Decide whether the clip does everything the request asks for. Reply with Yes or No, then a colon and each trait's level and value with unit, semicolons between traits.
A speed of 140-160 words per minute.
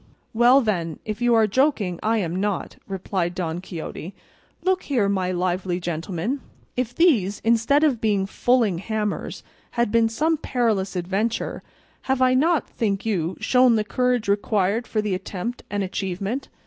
Yes: average, 155 wpm